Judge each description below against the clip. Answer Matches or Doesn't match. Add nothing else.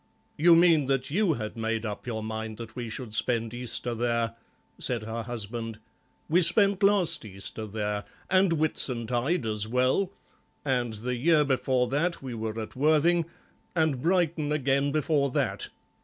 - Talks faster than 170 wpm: Doesn't match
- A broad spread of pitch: Matches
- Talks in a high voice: Doesn't match